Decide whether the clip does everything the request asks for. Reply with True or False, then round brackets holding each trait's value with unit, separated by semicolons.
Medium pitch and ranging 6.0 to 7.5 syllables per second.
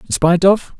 False (175 Hz; 5.5 syllables/s)